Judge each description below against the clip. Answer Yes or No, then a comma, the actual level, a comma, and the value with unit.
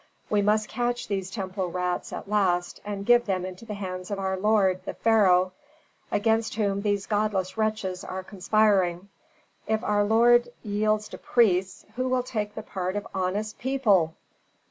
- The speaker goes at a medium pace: Yes, average, 165 wpm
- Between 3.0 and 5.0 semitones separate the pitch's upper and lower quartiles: No, narrow, 2.6 semitones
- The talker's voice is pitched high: Yes, high, 205 Hz